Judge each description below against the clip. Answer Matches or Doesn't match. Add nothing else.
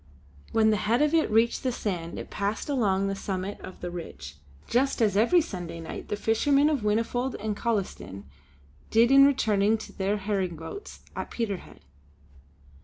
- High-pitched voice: Matches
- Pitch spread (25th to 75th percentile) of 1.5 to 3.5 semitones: Doesn't match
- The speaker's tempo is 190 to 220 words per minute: Doesn't match